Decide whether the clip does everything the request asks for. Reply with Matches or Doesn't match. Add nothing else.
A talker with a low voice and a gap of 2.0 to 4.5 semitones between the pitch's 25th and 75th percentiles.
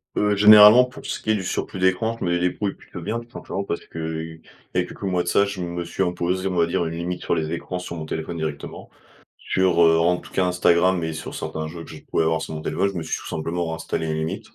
Matches